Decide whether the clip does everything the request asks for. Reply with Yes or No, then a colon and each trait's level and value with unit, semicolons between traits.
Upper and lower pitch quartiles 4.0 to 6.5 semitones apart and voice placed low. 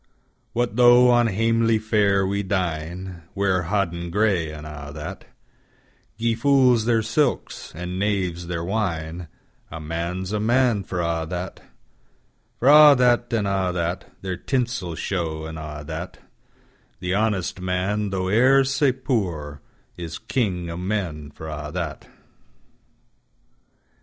Yes: average, 5.1 semitones; very low, 95 Hz